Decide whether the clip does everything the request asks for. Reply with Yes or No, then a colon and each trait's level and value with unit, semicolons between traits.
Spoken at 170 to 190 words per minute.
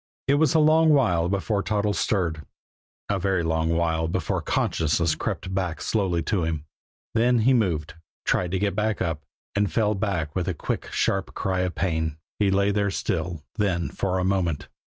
Yes: average, 175 wpm